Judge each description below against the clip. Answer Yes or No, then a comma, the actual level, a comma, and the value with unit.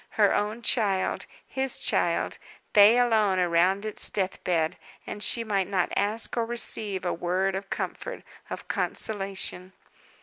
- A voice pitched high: Yes, high, 200 Hz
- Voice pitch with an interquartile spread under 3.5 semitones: Yes, average, 2.8 semitones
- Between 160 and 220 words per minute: No, average, 140 wpm